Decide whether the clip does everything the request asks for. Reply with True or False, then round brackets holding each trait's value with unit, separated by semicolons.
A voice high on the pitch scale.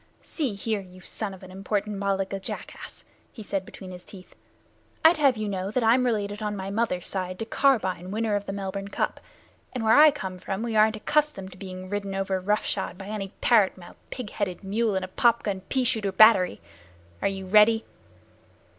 True (200 Hz)